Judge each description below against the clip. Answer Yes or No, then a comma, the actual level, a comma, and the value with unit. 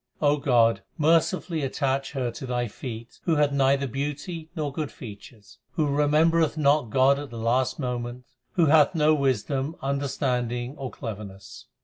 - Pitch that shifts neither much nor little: Yes, average, 3.5 semitones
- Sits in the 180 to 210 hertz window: No, low, 135 Hz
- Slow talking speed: No, average, 145 wpm